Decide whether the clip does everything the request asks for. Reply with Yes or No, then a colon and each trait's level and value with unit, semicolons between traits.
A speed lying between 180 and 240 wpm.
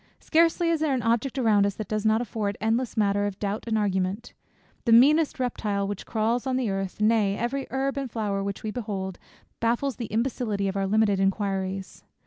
Yes: average, 195 wpm